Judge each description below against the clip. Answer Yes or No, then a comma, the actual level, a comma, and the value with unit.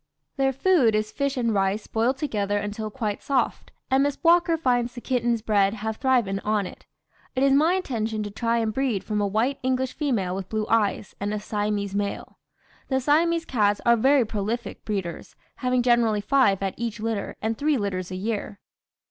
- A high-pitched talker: Yes, high, 225 Hz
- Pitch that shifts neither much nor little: Yes, average, 4.2 semitones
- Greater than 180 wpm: Yes, average, 190 wpm